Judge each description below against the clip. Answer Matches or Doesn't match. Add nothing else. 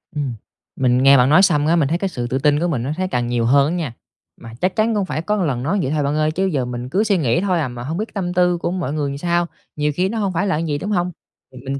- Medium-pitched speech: Matches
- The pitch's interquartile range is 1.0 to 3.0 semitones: Doesn't match